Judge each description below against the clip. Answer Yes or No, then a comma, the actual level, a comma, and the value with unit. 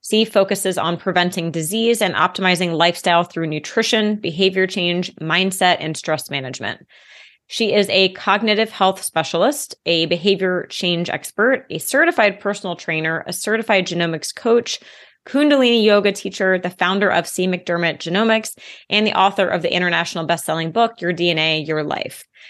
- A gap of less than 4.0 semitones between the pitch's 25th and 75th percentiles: Yes, average, 3.4 semitones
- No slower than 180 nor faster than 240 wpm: No, average, 145 wpm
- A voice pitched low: No, medium, 185 Hz